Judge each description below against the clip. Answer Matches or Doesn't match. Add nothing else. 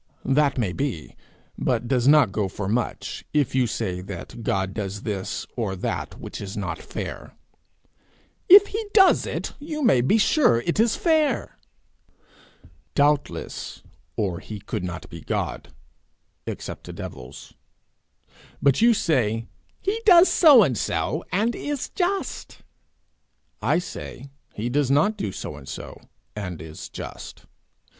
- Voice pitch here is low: Matches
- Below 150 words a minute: Matches